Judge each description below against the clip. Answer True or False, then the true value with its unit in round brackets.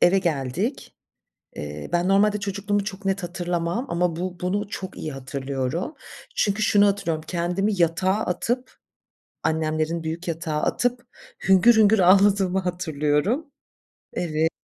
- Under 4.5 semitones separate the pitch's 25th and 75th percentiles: True (3.9 semitones)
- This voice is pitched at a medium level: True (180 Hz)